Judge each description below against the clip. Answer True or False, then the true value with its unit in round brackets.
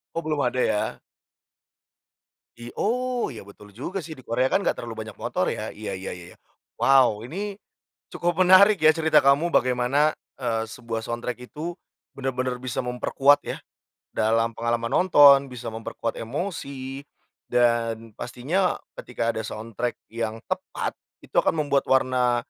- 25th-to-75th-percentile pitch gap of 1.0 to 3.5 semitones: False (4.4 semitones)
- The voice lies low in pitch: True (125 Hz)